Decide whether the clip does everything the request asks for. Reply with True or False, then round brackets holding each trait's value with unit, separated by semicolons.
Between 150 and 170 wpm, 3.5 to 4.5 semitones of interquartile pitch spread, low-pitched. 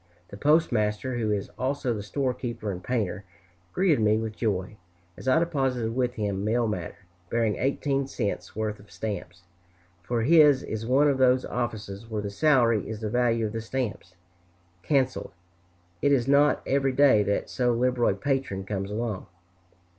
True (165 wpm; 3.9 semitones; 115 Hz)